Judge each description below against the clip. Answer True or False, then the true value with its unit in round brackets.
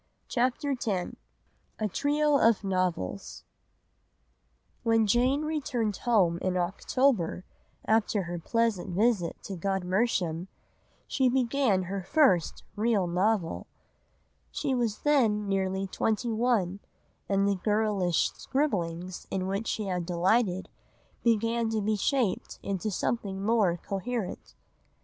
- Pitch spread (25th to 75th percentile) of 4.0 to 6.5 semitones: True (4.3 semitones)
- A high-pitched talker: True (205 Hz)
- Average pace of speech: False (115 wpm)